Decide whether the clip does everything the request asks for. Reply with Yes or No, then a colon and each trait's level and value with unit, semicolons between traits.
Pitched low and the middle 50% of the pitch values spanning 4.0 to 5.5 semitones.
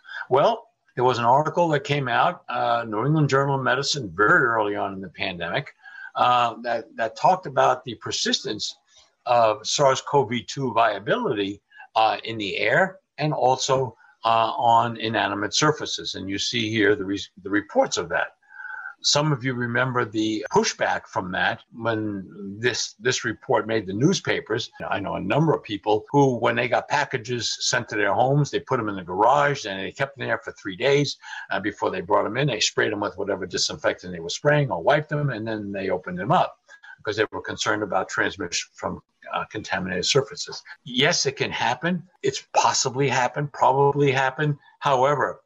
Yes: low, 130 Hz; average, 4.6 semitones